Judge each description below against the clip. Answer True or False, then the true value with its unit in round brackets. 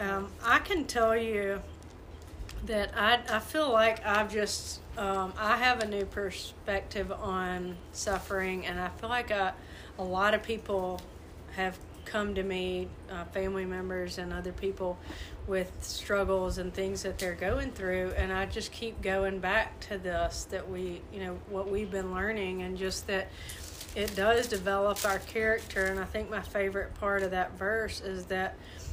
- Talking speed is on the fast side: False (165 wpm)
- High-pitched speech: True (195 Hz)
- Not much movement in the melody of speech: True (2.1 semitones)